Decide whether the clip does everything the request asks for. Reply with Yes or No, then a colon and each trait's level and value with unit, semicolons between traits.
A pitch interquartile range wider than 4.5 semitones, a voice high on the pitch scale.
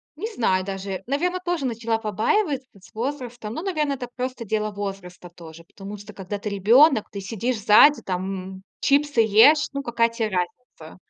Yes: wide, 5.5 semitones; high, 220 Hz